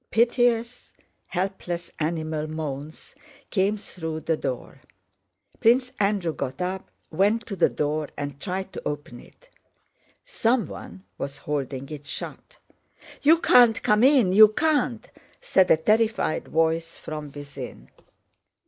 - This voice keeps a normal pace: No, slow, 120 wpm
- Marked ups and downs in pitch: Yes, wide, 6.6 semitones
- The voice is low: No, medium, 180 Hz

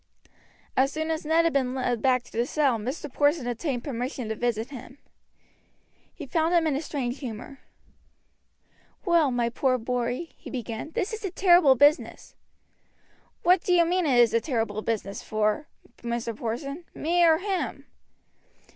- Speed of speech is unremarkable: Yes, average, 165 wpm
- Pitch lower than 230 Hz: No, very high, 265 Hz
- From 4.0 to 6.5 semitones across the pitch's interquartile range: Yes, average, 5.2 semitones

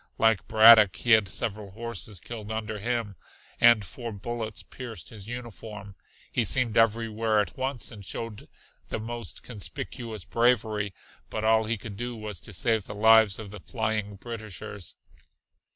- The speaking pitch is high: No, low, 110 Hz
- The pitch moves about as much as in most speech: No, narrow, 2.1 semitones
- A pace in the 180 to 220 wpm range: No, average, 150 wpm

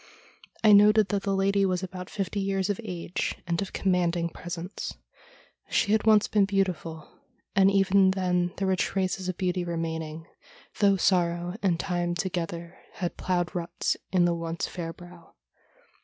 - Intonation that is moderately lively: No, narrow, 2.2 semitones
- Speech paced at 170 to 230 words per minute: No, average, 155 wpm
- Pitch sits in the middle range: Yes, medium, 180 Hz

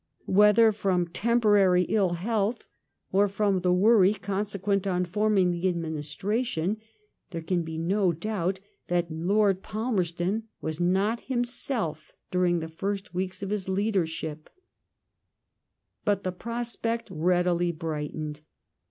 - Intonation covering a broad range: No, average, 3.3 semitones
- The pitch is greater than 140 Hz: Yes, high, 190 Hz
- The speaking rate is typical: No, slow, 115 wpm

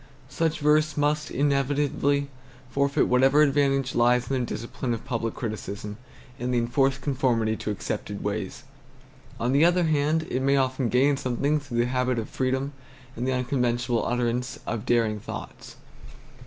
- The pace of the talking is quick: No, average, 155 wpm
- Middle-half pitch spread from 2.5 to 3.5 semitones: Yes, average, 3.0 semitones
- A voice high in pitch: No, low, 130 Hz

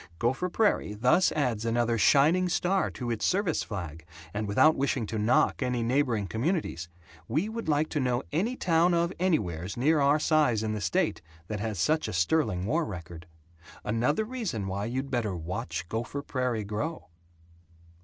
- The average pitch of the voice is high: No, low, 125 Hz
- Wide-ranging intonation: Yes, wide, 7.1 semitones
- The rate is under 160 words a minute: No, average, 165 wpm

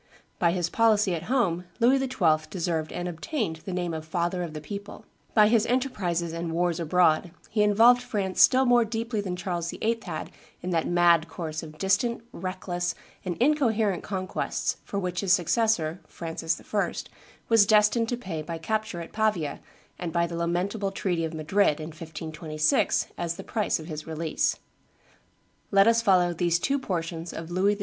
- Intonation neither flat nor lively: Yes, average, 4.3 semitones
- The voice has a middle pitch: Yes, medium, 180 Hz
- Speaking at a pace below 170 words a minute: No, average, 175 wpm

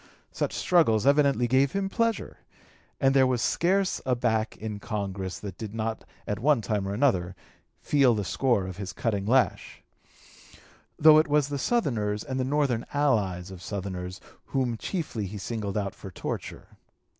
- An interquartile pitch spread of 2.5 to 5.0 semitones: No, wide, 5.6 semitones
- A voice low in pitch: Yes, low, 115 Hz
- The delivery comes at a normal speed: Yes, average, 165 wpm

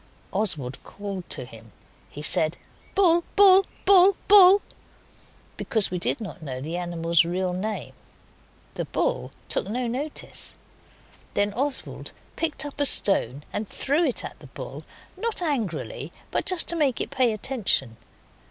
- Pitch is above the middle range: Yes, high, 220 Hz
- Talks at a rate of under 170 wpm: Yes, average, 145 wpm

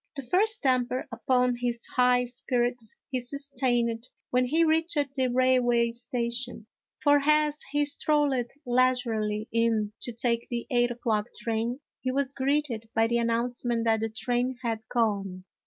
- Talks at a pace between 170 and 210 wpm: No, average, 150 wpm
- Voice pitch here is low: No, high, 245 Hz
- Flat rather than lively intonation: Yes, narrow, 2.0 semitones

